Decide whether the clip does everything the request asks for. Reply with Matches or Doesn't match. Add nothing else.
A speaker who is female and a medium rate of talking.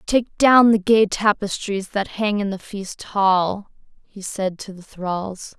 Matches